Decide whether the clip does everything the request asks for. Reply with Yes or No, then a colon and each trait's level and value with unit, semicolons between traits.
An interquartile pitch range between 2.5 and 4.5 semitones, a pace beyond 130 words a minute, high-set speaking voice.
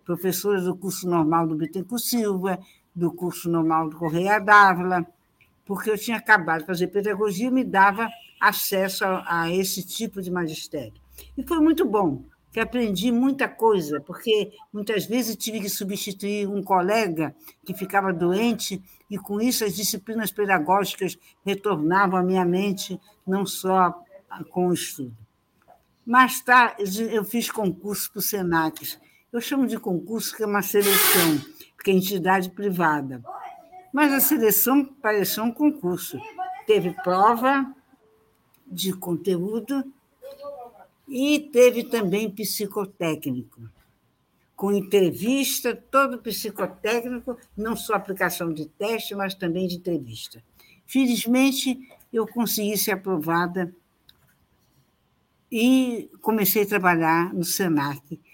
No: average, 4.1 semitones; average, 125 wpm; high, 200 Hz